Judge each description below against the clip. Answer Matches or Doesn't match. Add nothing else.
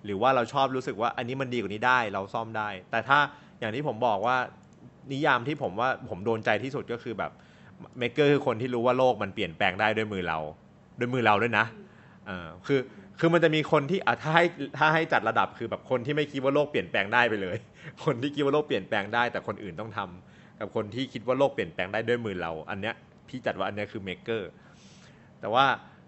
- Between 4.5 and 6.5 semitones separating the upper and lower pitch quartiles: Matches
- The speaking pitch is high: Doesn't match